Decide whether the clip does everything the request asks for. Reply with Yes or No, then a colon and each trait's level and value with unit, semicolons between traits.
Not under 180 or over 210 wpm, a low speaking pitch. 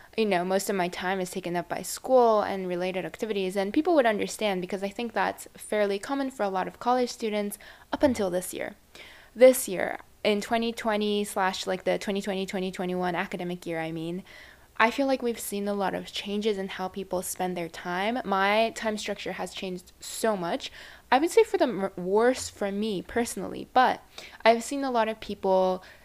No: average, 195 wpm; high, 200 Hz